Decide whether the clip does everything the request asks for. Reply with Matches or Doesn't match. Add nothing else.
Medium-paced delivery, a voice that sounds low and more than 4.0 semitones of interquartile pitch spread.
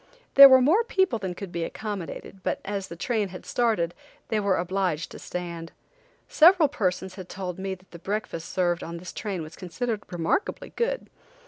Doesn't match